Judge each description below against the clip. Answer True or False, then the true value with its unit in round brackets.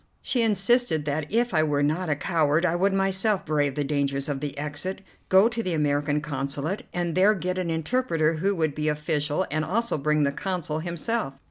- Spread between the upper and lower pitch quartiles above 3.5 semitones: True (4.4 semitones)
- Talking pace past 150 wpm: True (200 wpm)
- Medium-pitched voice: True (160 Hz)